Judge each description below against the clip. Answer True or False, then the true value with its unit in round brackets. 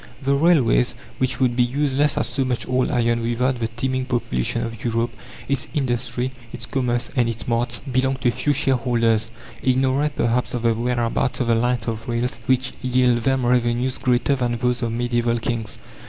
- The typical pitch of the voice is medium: False (125 Hz)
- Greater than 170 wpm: True (185 wpm)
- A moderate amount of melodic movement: False (1.8 semitones)